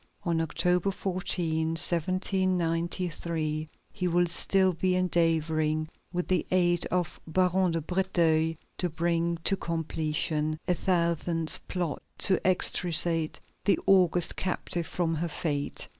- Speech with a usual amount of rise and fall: No, narrow, 2.1 semitones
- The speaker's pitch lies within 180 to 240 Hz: No, medium, 170 Hz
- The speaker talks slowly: Yes, slow, 115 wpm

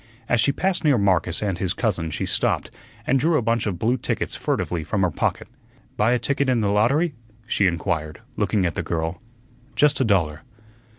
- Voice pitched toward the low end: Yes, low, 105 Hz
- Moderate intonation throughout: No, wide, 6.3 semitones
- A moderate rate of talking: Yes, average, 195 wpm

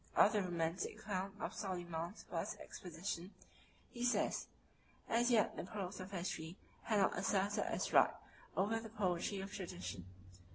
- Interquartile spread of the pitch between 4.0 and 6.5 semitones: No, average, 2.9 semitones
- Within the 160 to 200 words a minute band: No, average, 150 wpm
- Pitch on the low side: No, high, 190 Hz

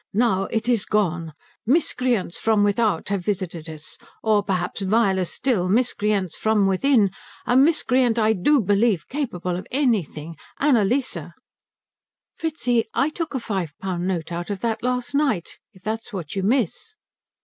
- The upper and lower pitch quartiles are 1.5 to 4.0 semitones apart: No, average, 4.9 semitones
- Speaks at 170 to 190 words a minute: No, average, 150 wpm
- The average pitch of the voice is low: No, high, 210 Hz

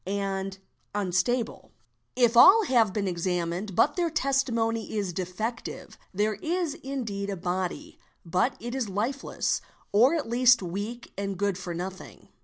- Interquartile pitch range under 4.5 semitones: No, average, 4.9 semitones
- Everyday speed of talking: Yes, average, 155 wpm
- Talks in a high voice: Yes, high, 210 Hz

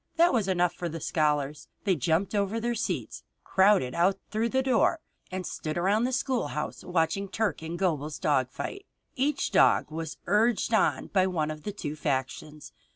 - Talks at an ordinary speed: Yes, average, 175 wpm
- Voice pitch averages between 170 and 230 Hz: Yes, medium, 185 Hz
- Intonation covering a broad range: Yes, wide, 6.1 semitones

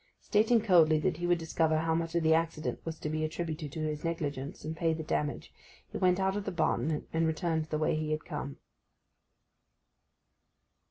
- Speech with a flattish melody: Yes, narrow, 1.6 semitones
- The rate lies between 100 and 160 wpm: No, average, 195 wpm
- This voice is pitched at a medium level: Yes, medium, 160 Hz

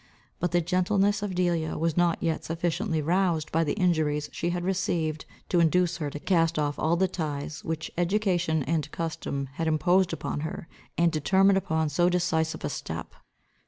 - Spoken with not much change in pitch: Yes, narrow, 2.3 semitones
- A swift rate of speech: No, average, 175 wpm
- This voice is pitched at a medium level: Yes, medium, 170 Hz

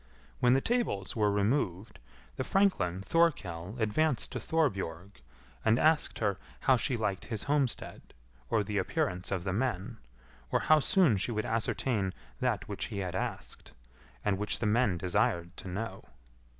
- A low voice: Yes, low, 105 Hz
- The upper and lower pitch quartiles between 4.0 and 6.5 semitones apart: Yes, average, 5.3 semitones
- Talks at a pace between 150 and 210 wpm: Yes, average, 155 wpm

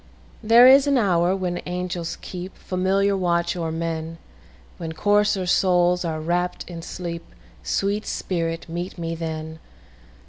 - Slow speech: Yes, slow, 115 wpm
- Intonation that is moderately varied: No, narrow, 2.3 semitones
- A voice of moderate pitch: Yes, medium, 175 Hz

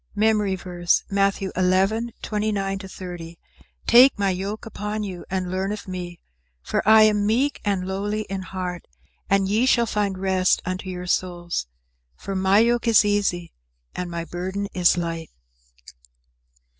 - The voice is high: Yes, high, 195 Hz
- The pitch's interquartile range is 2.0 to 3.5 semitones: Yes, narrow, 2.4 semitones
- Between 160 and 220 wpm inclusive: No, average, 145 wpm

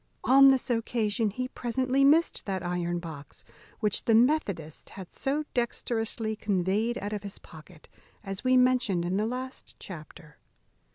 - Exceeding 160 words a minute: No, average, 150 wpm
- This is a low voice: No, high, 220 Hz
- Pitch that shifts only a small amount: No, average, 5.3 semitones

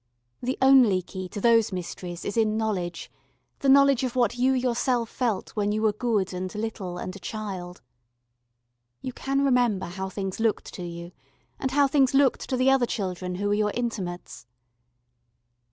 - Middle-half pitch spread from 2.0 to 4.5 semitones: No, average, 5.1 semitones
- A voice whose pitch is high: Yes, high, 215 Hz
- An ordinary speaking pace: Yes, average, 170 wpm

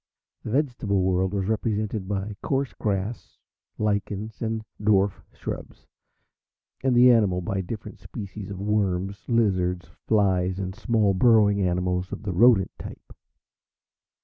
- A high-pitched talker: No, low, 100 Hz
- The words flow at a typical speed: No, slow, 125 wpm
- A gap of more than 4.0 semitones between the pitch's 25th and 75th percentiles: No, average, 2.7 semitones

